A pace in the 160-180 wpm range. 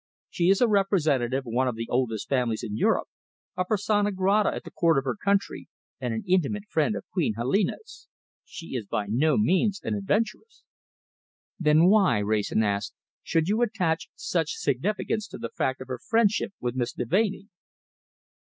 Yes: average, 170 wpm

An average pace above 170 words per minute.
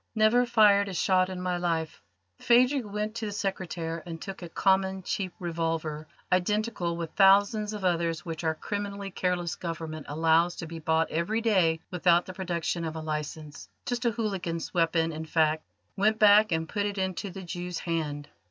Yes: average, 180 wpm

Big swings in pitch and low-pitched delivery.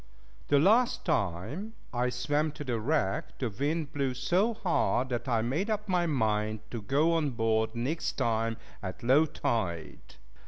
Yes: wide, 6.0 semitones; low, 130 Hz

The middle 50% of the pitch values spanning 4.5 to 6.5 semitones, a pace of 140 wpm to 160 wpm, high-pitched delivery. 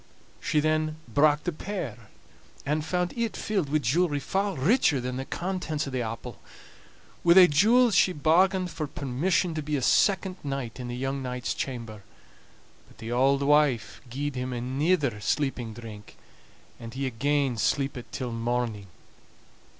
No: average, 5.2 semitones; average, 155 wpm; medium, 140 Hz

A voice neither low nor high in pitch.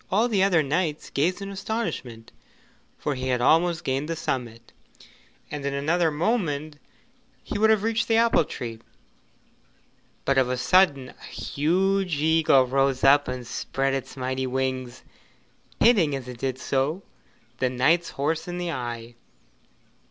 Yes: medium, 145 Hz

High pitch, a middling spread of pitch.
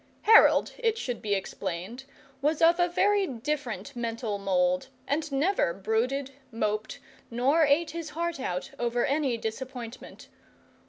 No: very high, 260 Hz; wide, 5.9 semitones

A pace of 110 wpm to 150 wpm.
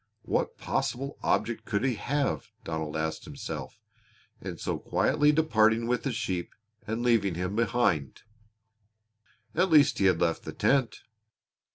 Yes: average, 140 wpm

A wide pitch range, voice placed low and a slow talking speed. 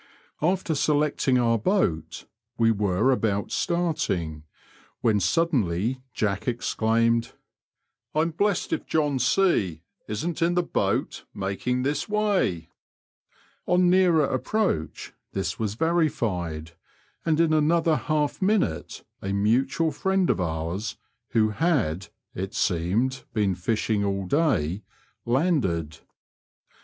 Yes: wide, 8.9 semitones; low, 120 Hz; slow, 110 wpm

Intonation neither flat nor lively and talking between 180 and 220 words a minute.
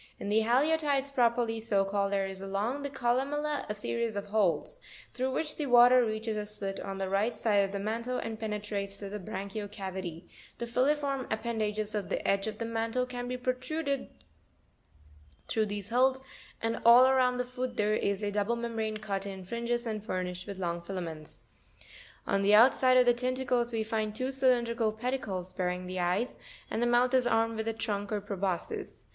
Yes: average, 3.8 semitones; average, 190 wpm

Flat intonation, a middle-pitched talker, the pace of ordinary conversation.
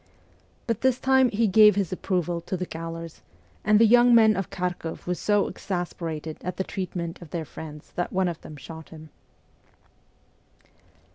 No: average, 4.1 semitones; medium, 180 Hz; average, 165 wpm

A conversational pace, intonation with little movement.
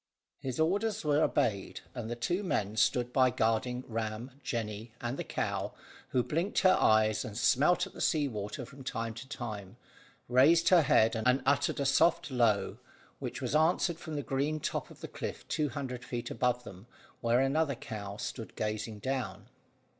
No: average, 175 wpm; average, 4.9 semitones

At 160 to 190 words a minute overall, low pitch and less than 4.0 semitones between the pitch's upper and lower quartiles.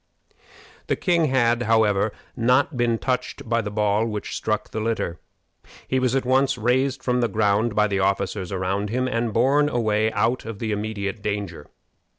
Yes: average, 170 wpm; low, 115 Hz; average, 3.3 semitones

